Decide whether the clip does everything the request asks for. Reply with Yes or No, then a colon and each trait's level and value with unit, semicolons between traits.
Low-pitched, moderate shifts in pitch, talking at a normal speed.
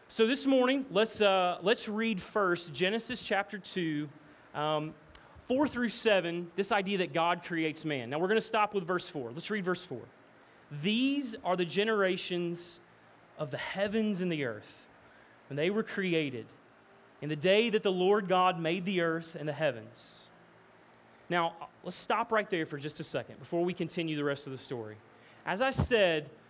No: medium, 180 Hz; average, 4.9 semitones; average, 180 wpm